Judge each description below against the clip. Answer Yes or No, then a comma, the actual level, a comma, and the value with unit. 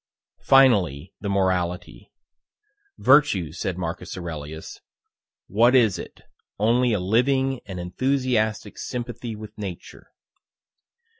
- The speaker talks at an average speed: No, slow, 95 wpm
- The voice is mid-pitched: No, low, 105 Hz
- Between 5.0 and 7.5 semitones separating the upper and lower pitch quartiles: Yes, wide, 5.5 semitones